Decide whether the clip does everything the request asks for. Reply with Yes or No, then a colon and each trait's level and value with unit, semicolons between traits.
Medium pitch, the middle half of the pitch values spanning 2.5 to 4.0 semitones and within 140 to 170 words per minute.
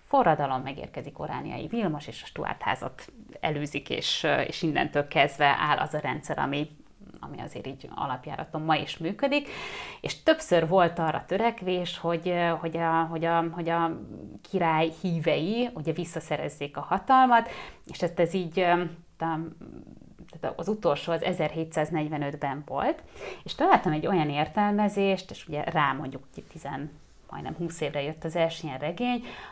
Yes: medium, 165 Hz; average, 2.9 semitones; average, 145 wpm